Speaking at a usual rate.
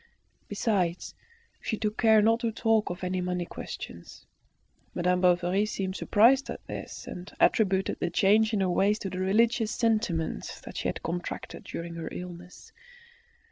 Yes: average, 150 wpm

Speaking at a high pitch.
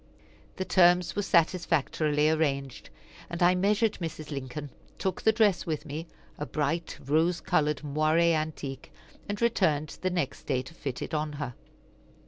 No: medium, 155 Hz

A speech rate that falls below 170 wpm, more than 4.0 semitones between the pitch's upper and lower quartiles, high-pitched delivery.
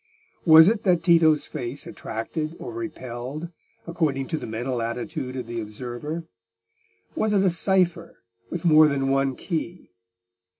No: average, 140 wpm; average, 5.1 semitones; medium, 155 Hz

